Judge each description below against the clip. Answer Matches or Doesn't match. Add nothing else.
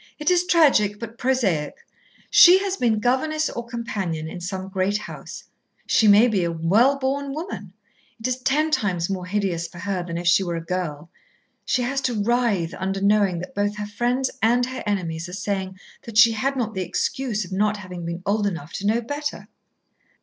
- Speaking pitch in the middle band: Doesn't match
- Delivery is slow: Doesn't match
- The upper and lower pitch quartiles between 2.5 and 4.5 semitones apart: Doesn't match